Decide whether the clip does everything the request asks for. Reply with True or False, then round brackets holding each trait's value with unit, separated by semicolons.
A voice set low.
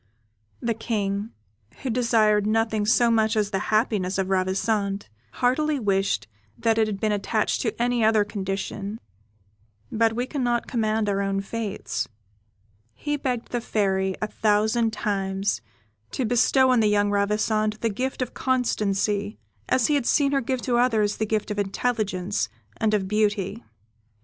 False (215 Hz)